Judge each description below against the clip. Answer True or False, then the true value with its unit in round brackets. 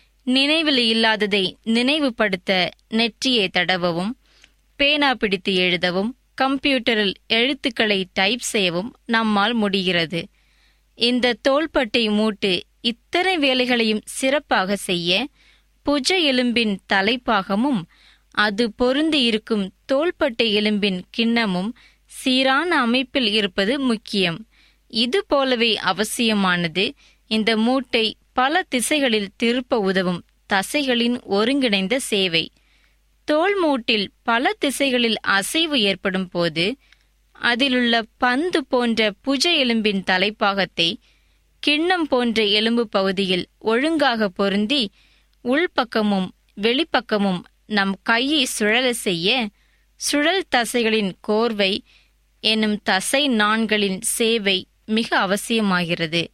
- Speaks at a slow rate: False (85 wpm)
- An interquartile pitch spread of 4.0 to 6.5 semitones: True (4.6 semitones)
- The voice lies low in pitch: False (225 Hz)